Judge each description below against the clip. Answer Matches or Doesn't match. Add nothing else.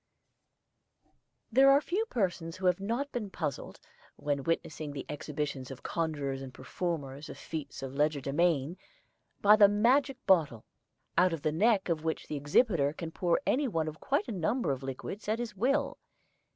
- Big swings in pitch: Matches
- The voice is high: Doesn't match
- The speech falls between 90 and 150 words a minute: Doesn't match